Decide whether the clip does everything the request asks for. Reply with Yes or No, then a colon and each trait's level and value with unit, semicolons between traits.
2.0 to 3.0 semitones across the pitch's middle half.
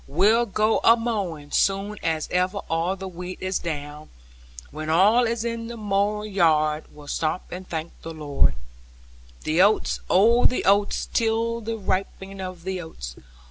No: average, 4.8 semitones